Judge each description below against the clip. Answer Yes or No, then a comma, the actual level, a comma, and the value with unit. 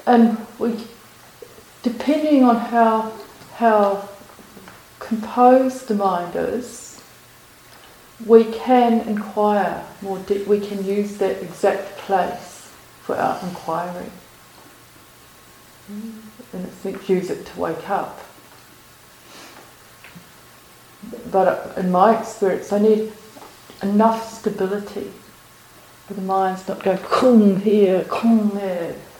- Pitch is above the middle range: Yes, high, 205 Hz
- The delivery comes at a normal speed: No, slow, 100 wpm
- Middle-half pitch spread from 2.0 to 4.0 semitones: Yes, average, 2.9 semitones